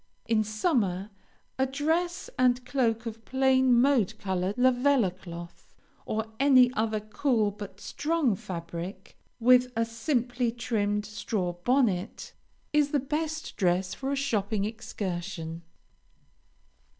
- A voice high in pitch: Yes, high, 225 Hz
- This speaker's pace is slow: Yes, slow, 115 wpm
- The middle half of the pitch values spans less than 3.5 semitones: No, average, 4.9 semitones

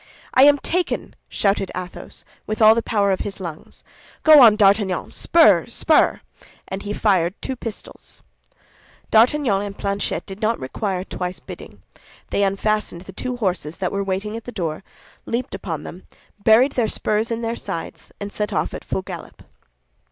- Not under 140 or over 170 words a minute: Yes, average, 165 wpm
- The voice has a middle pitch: No, high, 205 Hz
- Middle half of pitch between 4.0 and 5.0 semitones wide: No, average, 3.3 semitones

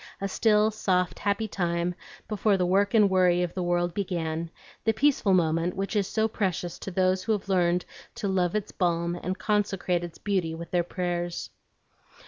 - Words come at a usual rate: Yes, average, 180 wpm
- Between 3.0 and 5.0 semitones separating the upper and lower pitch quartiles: No, narrow, 2.6 semitones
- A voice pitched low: No, medium, 185 Hz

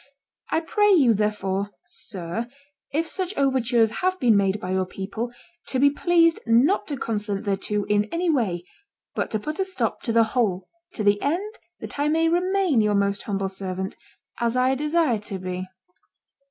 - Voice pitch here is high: Yes, high, 230 Hz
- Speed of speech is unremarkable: Yes, average, 175 wpm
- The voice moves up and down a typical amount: No, wide, 7.6 semitones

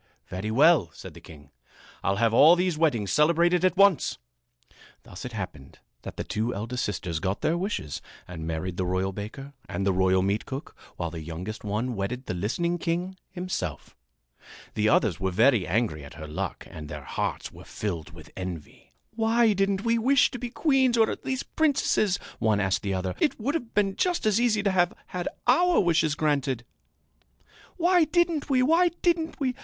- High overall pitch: No, low, 135 Hz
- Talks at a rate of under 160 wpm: No, average, 185 wpm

